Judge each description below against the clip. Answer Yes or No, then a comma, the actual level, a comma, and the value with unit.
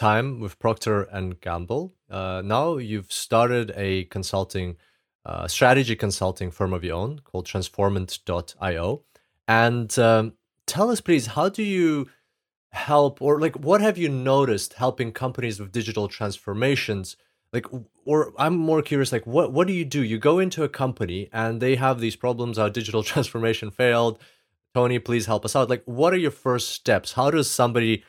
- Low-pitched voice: Yes, low, 120 Hz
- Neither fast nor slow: Yes, average, 170 wpm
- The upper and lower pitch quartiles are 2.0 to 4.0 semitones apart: No, average, 4.9 semitones